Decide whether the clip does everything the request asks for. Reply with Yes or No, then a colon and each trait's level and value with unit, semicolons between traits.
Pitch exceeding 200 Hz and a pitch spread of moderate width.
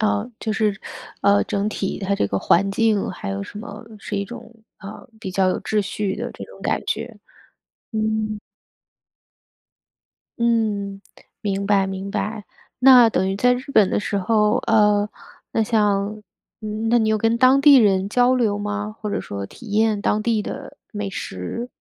No: high, 210 Hz; narrow, 2.1 semitones